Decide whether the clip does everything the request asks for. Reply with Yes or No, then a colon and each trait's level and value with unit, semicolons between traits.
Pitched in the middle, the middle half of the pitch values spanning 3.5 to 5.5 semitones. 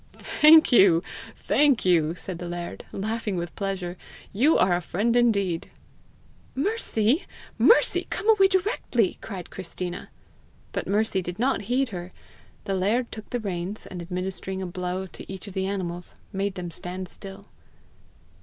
No: high, 195 Hz; average, 4.4 semitones